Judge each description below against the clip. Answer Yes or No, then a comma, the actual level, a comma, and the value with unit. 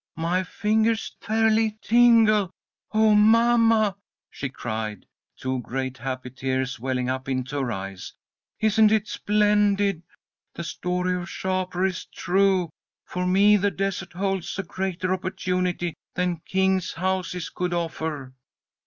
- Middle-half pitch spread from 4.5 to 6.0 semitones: Yes, wide, 5.6 semitones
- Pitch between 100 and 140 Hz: No, medium, 185 Hz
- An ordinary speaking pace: No, slow, 125 wpm